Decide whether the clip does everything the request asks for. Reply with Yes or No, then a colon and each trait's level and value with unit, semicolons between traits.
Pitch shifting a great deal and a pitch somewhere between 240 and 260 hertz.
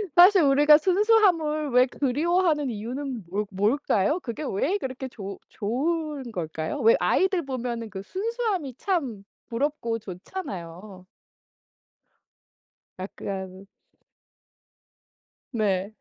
Yes: wide, 7.4 semitones; very high, 255 Hz